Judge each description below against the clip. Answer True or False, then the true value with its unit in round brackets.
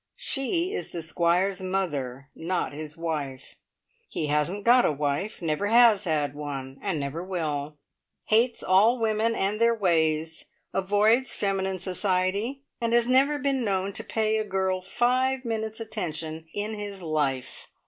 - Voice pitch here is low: False (190 Hz)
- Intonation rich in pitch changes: True (5.8 semitones)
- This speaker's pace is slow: False (150 wpm)